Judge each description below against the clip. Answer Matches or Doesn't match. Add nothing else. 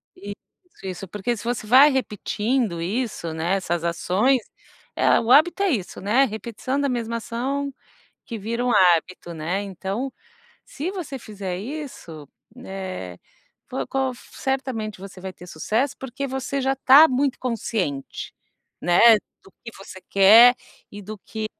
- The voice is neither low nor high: Doesn't match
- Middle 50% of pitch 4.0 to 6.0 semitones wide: Matches